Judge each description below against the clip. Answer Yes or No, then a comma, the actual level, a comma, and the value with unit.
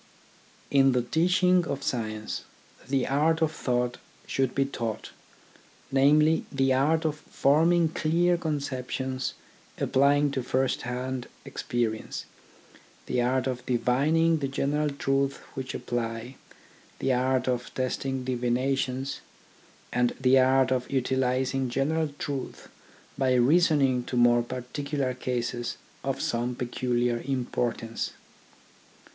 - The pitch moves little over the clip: Yes, narrow, 2.3 semitones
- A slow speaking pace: Yes, slow, 115 wpm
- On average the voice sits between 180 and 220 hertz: No, low, 130 Hz